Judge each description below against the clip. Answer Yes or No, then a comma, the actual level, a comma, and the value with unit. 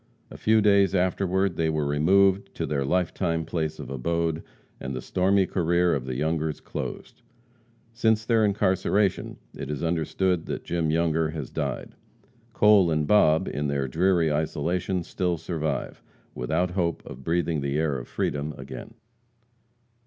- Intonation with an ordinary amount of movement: Yes, average, 3.6 semitones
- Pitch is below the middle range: Yes, very low, 85 Hz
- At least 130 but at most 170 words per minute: Yes, average, 155 wpm